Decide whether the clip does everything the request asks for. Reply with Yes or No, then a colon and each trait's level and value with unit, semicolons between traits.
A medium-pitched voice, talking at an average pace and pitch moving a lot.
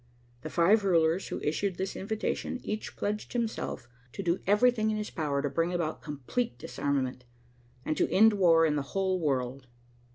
Yes: medium, 175 Hz; average, 170 wpm; wide, 6.0 semitones